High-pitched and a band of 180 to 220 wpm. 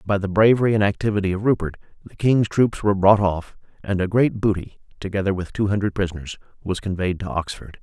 No: low, 100 Hz; average, 200 wpm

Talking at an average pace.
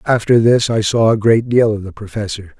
No: fast, 230 wpm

